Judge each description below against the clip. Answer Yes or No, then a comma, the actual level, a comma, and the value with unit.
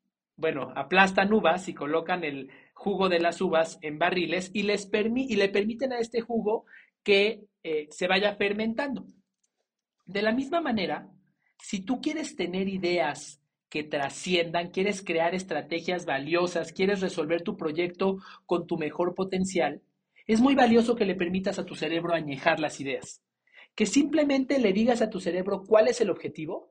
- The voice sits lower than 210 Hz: Yes, high, 190 Hz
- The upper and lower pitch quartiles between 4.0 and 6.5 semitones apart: Yes, average, 4.6 semitones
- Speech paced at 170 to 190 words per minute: No, average, 160 wpm